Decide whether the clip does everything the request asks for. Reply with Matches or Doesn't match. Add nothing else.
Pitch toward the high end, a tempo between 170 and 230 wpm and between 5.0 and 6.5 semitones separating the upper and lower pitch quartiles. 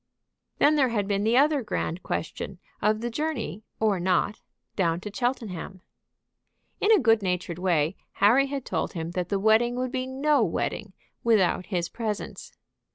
Doesn't match